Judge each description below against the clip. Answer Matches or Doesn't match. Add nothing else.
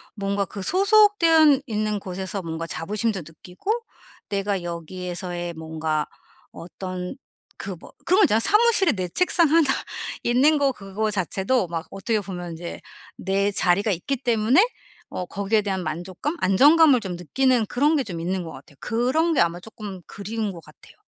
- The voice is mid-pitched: Doesn't match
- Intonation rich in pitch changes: Matches